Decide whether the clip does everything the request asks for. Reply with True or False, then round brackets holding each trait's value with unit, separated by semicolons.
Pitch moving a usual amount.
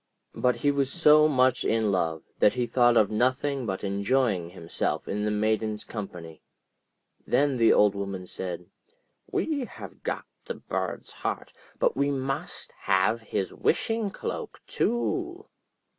False (6.1 semitones)